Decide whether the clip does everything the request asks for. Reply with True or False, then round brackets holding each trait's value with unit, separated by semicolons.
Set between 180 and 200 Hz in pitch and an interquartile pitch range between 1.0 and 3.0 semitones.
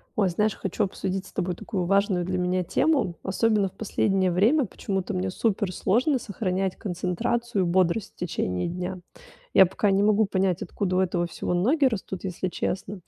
True (190 Hz; 2.5 semitones)